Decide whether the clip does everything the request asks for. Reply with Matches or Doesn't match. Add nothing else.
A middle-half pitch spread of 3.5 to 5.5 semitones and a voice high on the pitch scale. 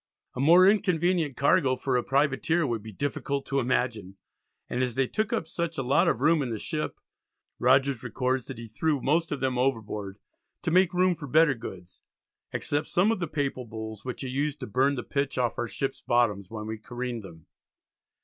Doesn't match